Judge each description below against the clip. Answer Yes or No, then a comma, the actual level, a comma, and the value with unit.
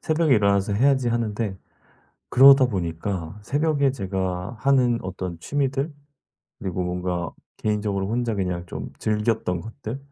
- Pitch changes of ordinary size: No, wide, 5.9 semitones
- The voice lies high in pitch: No, low, 105 Hz